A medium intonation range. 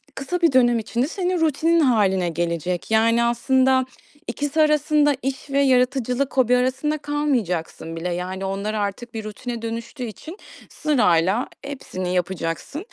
No: wide, 6.5 semitones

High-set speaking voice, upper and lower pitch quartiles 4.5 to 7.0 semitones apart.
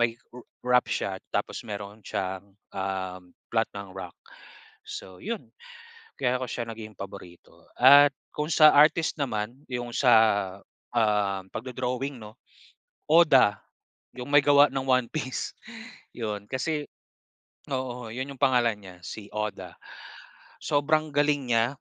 No: low, 120 Hz; average, 5.0 semitones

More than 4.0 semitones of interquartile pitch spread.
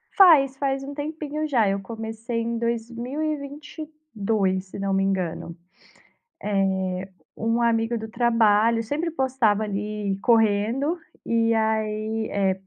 Yes: average, 4.6 semitones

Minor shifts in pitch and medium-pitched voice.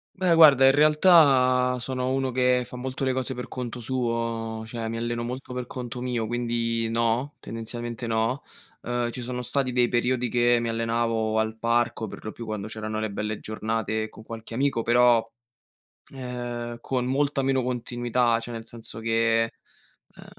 No: narrow, 1.9 semitones; low, 120 Hz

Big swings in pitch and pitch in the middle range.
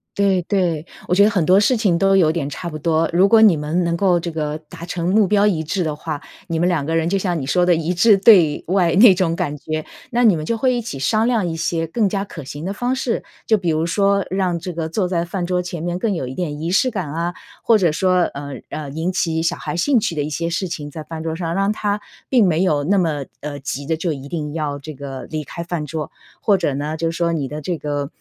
No: average, 3.7 semitones; medium, 170 Hz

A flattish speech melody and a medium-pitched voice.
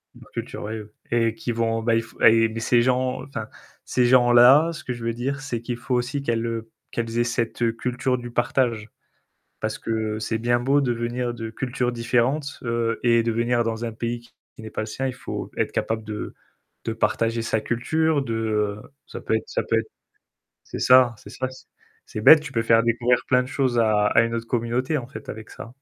No: narrow, 1.7 semitones; low, 120 Hz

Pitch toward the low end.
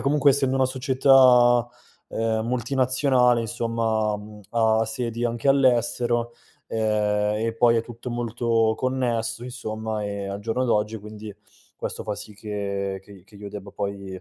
Yes: low, 115 Hz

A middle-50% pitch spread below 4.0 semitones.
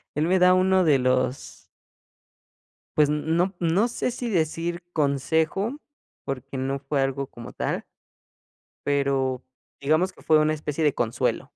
No: average, 4.3 semitones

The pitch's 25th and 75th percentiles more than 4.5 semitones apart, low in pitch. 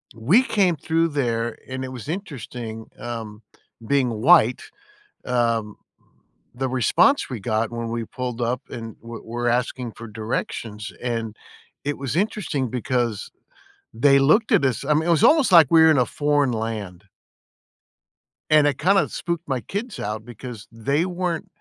Yes: wide, 5.6 semitones; low, 125 Hz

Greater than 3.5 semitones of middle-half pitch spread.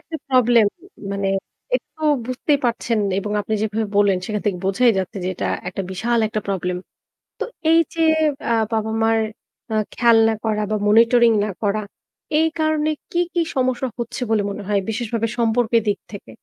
No: average, 2.8 semitones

